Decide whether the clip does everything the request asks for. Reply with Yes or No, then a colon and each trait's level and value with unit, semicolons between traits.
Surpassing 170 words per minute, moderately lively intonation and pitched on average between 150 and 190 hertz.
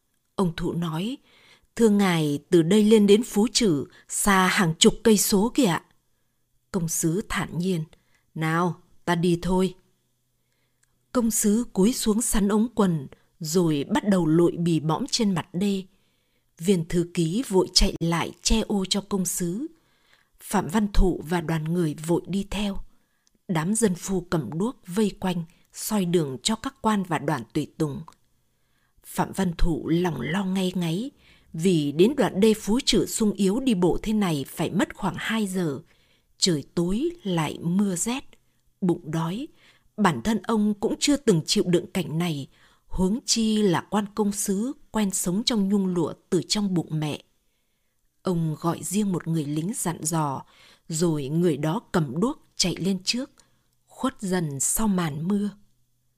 No: slow, 165 wpm; average, 4.3 semitones; medium, 185 Hz